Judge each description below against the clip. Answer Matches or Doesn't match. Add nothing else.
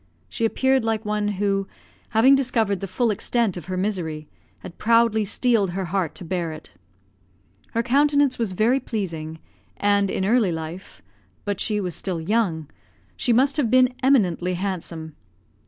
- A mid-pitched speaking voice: Doesn't match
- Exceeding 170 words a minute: Doesn't match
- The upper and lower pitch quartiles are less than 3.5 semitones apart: Doesn't match